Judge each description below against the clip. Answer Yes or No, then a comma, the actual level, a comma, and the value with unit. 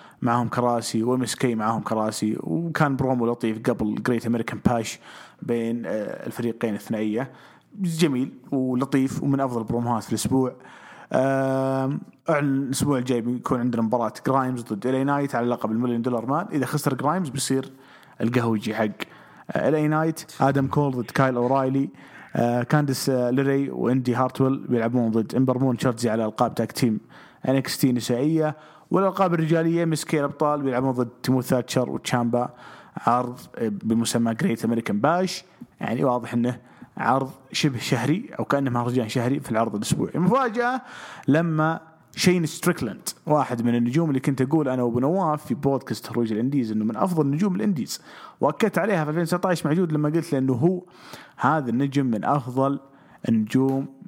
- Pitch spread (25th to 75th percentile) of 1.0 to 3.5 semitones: No, average, 3.9 semitones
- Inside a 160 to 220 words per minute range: No, average, 140 wpm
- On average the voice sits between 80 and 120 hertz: No, low, 130 Hz